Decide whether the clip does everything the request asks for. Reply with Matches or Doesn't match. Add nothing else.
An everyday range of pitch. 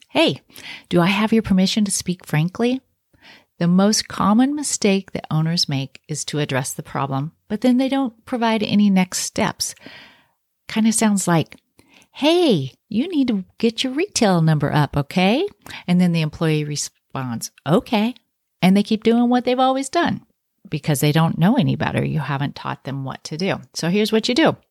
Doesn't match